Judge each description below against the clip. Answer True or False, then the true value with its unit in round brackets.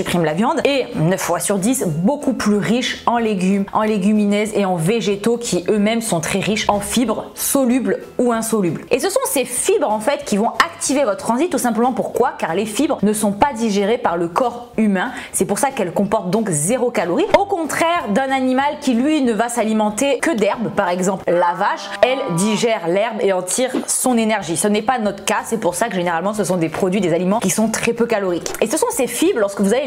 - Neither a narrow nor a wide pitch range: True (4.3 semitones)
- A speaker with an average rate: False (230 wpm)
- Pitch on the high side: True (220 Hz)